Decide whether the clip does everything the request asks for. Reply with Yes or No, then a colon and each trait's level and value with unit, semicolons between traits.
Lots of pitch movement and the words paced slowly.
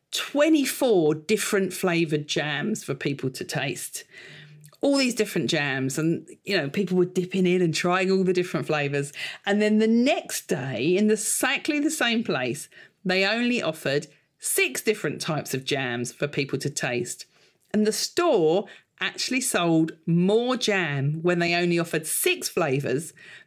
No: wide, 6.1 semitones; average, 155 wpm